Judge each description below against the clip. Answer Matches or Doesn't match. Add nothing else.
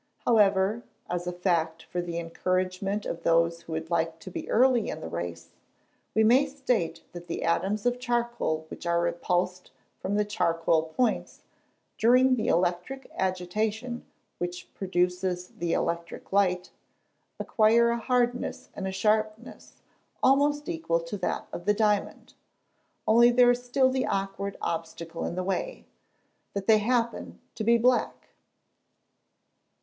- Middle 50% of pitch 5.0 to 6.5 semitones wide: Matches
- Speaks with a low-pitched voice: Doesn't match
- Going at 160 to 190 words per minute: Doesn't match